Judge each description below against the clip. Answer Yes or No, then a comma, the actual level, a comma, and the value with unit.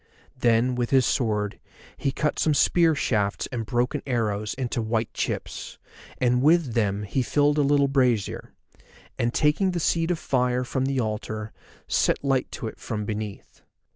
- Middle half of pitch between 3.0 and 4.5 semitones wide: Yes, average, 4.1 semitones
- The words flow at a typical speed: Yes, average, 165 wpm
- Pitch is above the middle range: No, low, 125 Hz